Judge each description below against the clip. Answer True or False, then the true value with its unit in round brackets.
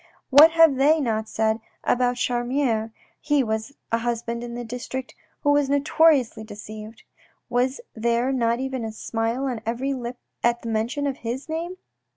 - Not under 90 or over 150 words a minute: False (165 wpm)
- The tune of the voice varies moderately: True (3.2 semitones)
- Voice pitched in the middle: False (245 Hz)